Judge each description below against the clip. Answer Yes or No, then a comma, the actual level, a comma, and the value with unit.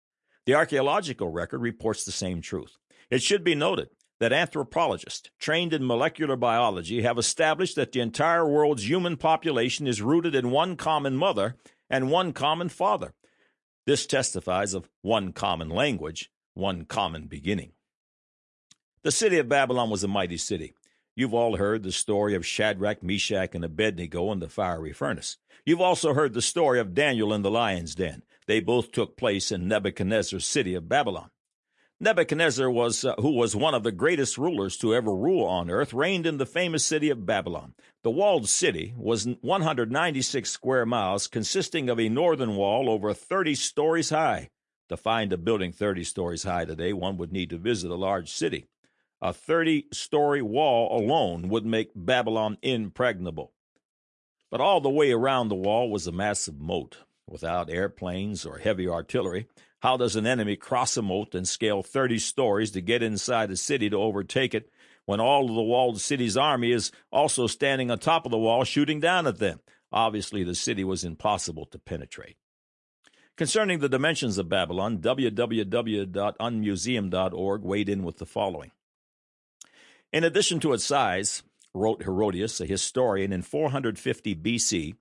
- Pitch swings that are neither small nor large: No, wide, 5.7 semitones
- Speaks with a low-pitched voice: Yes, low, 110 Hz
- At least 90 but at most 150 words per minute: No, average, 165 wpm